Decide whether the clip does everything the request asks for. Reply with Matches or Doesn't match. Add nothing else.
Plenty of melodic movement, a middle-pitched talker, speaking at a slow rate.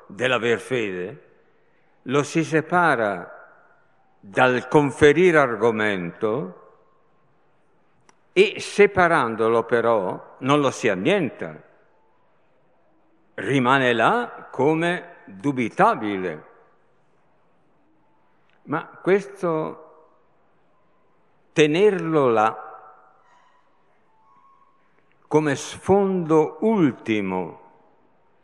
Matches